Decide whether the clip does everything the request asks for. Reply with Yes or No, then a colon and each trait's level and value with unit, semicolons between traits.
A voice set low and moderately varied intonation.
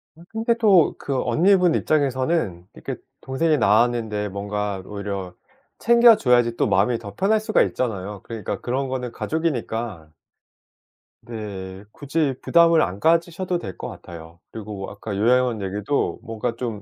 No: low, 120 Hz; wide, 7.4 semitones